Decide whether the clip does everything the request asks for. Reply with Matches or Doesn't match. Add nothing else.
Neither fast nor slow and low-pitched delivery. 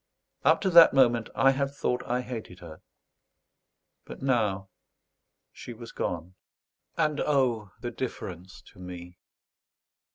Doesn't match